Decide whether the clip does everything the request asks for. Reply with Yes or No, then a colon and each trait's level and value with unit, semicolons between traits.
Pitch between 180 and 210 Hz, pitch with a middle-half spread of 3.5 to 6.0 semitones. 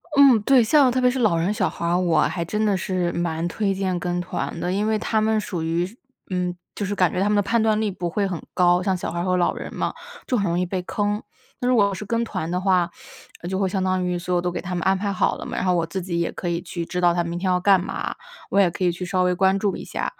No: medium, 185 Hz; average, 2.7 semitones